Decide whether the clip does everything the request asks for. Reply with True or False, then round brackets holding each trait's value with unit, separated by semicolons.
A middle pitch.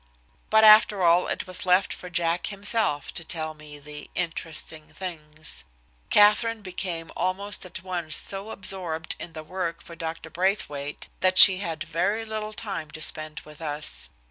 True (175 Hz)